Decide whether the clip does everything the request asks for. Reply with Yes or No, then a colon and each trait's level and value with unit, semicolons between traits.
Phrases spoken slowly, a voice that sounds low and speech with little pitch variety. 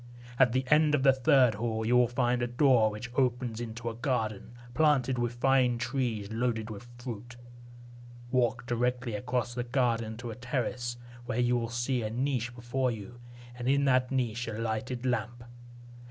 No: average, 175 wpm; low, 120 Hz; narrow, 1.6 semitones